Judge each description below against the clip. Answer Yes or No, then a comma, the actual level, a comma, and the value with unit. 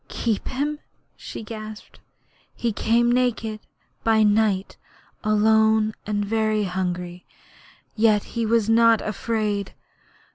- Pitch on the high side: Yes, high, 220 Hz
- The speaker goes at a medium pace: No, slow, 105 wpm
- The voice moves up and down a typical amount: No, narrow, 1.6 semitones